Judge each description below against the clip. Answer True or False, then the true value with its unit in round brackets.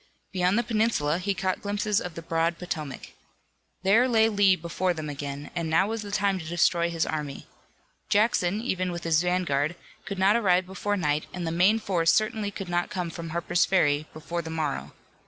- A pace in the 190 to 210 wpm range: True (195 wpm)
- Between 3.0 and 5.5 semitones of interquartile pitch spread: True (3.7 semitones)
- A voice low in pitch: False (180 Hz)